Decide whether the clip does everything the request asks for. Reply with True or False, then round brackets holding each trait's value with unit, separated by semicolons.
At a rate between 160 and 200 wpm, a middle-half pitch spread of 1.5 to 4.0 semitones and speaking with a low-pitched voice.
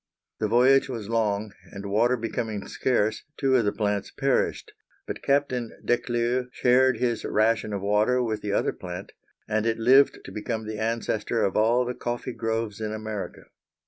True (170 wpm; 2.6 semitones; 115 Hz)